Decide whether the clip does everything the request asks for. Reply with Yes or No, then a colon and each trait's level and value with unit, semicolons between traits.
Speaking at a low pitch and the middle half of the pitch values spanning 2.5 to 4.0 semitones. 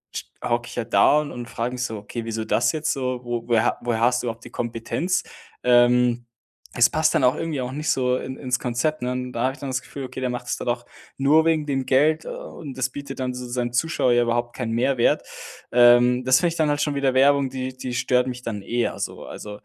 No: low, 125 Hz; narrow, 2.1 semitones